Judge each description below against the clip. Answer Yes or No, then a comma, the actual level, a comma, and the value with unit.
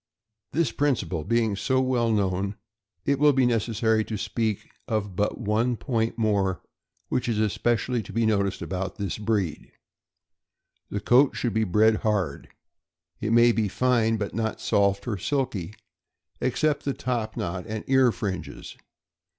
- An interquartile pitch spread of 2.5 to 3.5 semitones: Yes, average, 3.2 semitones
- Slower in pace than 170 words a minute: Yes, average, 150 wpm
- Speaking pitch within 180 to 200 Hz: No, low, 110 Hz